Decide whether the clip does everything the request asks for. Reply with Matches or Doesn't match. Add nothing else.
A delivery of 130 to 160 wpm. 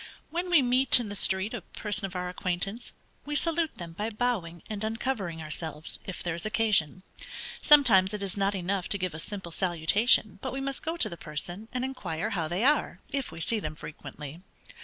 Doesn't match